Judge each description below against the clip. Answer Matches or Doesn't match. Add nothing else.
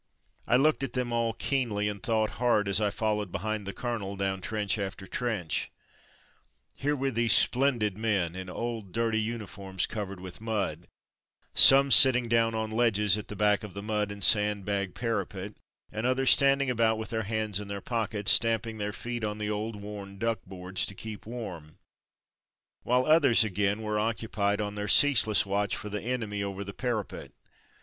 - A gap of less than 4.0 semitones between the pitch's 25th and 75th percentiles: Matches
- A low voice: Matches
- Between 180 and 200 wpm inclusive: Matches